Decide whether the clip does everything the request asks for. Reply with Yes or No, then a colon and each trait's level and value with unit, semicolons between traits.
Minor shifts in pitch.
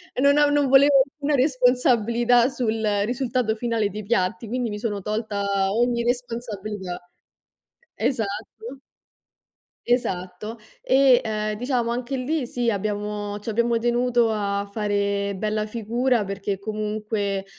No: average, 3.1 semitones